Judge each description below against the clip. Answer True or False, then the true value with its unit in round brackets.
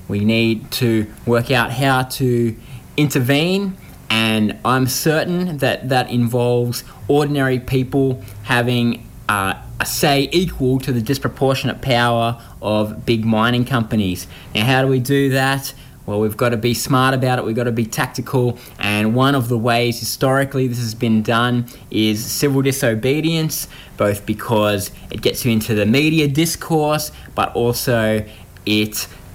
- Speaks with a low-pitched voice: True (120 Hz)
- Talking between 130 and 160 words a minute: True (150 wpm)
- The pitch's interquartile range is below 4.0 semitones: True (3.3 semitones)